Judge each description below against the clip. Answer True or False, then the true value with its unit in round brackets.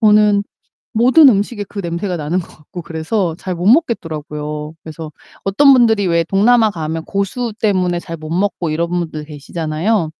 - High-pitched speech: False (180 Hz)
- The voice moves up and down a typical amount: True (4.7 semitones)